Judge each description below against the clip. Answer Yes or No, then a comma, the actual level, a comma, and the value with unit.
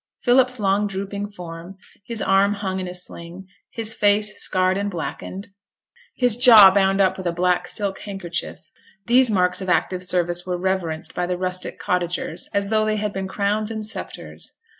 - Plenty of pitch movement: No, narrow, 2.5 semitones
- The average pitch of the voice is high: Yes, high, 195 Hz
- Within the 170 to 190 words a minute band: Yes, average, 175 wpm